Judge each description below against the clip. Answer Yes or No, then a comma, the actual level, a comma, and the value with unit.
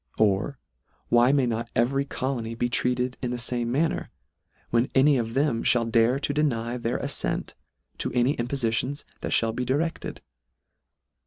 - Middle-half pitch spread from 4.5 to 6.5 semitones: No, average, 2.7 semitones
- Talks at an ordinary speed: Yes, average, 160 wpm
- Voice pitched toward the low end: Yes, low, 125 Hz